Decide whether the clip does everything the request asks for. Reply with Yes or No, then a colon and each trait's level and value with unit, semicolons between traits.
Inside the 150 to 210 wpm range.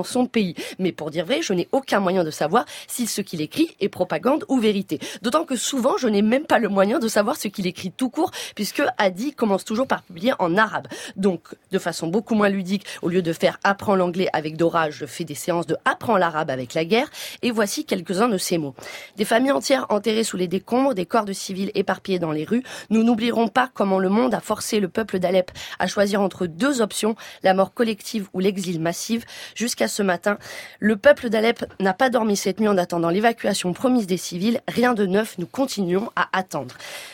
No: fast, 220 wpm